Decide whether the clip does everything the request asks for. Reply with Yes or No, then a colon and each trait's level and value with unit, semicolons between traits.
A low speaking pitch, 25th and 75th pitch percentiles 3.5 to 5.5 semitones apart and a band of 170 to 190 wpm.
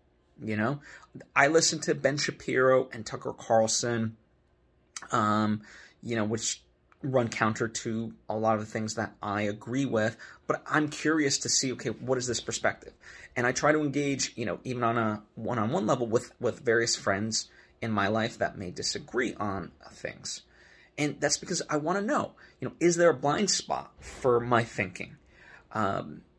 Yes: low, 115 Hz; average, 4.5 semitones; average, 175 wpm